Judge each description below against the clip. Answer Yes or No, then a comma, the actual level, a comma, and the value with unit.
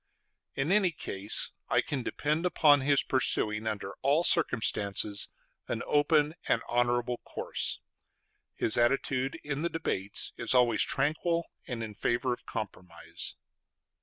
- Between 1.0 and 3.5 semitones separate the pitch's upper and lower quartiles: No, average, 5.2 semitones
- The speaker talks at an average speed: No, slow, 130 wpm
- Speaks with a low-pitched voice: Yes, low, 130 Hz